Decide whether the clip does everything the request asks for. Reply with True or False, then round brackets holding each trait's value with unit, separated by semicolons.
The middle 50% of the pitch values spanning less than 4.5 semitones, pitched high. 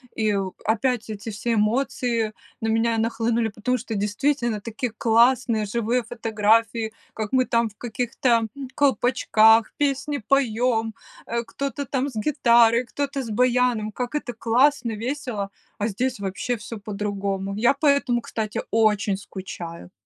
True (2.8 semitones; 230 Hz)